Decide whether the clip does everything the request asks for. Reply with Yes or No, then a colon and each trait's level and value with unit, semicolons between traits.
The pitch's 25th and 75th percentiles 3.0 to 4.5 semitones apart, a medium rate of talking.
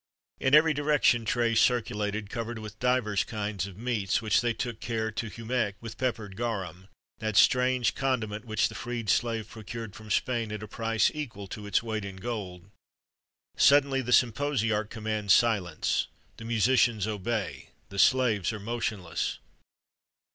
No: narrow, 2.5 semitones; average, 160 wpm